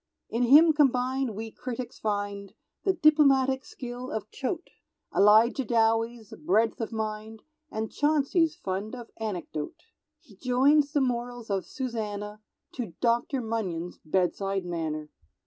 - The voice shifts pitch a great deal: No, average, 4.1 semitones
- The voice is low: No, high, 230 Hz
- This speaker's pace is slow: Yes, slow, 130 wpm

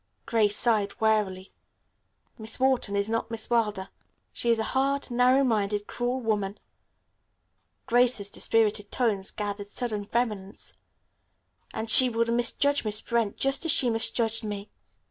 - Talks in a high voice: Yes, high, 225 Hz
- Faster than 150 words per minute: No, slow, 135 wpm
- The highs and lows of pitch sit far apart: No, average, 2.7 semitones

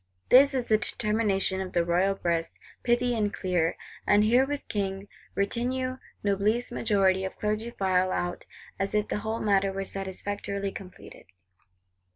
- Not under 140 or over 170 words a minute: Yes, average, 145 wpm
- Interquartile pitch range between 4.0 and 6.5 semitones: No, average, 3.0 semitones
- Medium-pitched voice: No, high, 200 Hz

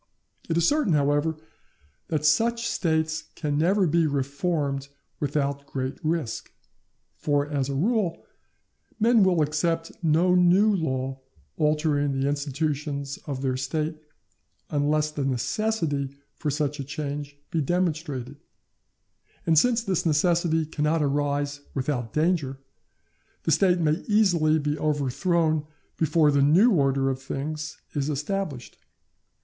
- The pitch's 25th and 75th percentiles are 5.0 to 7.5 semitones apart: No, average, 2.9 semitones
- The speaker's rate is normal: No, slow, 125 wpm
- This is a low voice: No, medium, 150 Hz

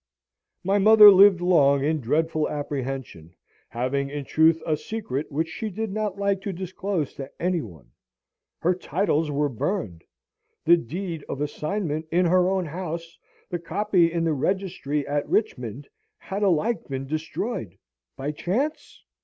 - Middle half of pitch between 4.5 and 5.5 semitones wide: Yes, average, 5.0 semitones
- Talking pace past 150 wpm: No, average, 145 wpm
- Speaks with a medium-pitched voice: Yes, medium, 165 Hz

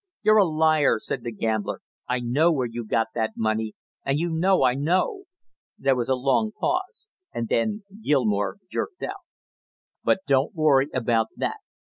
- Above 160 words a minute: Yes, average, 170 wpm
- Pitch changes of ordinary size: No, wide, 6.9 semitones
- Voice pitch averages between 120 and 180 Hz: Yes, low, 135 Hz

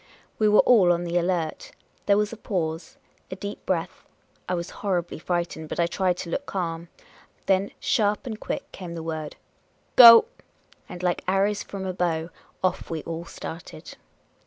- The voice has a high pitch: No, medium, 180 Hz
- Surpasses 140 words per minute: Yes, average, 180 wpm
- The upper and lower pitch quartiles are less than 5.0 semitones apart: Yes, average, 3.0 semitones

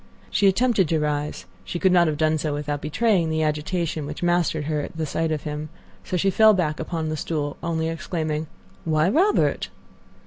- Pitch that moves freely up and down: No, average, 2.7 semitones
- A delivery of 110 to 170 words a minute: No, average, 185 wpm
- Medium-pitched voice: Yes, medium, 160 Hz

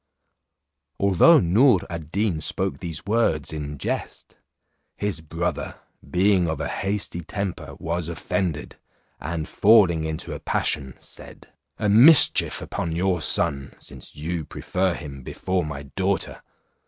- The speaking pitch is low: Yes, very low, 85 Hz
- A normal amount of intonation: Yes, average, 4.1 semitones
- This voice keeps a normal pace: No, slow, 130 wpm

